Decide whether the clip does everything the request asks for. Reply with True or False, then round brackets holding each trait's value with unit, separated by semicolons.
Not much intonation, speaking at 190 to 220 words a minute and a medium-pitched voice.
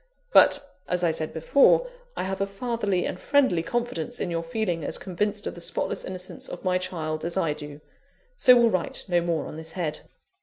False (3.8 semitones; 200 wpm; 180 Hz)